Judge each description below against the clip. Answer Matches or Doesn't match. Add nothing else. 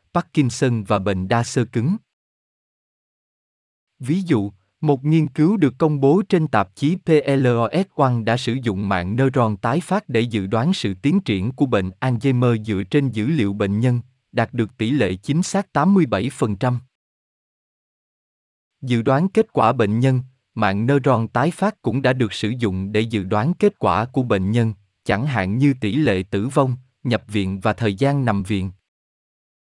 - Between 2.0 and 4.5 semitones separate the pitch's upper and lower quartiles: Doesn't match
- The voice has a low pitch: Matches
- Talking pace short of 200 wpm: Matches